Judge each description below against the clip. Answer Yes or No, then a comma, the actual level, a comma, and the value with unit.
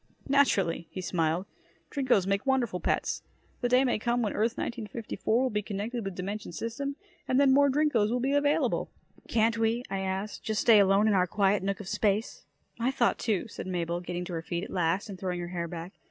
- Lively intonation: No, average, 4.6 semitones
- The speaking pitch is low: No, high, 210 Hz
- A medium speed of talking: No, fast, 210 wpm